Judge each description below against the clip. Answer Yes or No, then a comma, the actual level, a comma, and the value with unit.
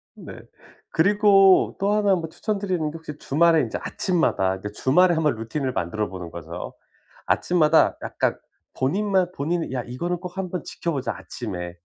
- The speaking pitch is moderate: Yes, medium, 160 Hz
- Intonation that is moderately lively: No, wide, 6.8 semitones